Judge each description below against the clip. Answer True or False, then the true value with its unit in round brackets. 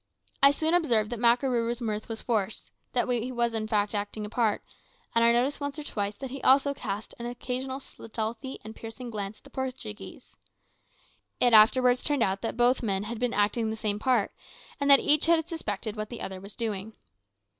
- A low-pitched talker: False (235 Hz)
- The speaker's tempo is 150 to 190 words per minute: False (200 wpm)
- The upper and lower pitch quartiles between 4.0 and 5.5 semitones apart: False (3.3 semitones)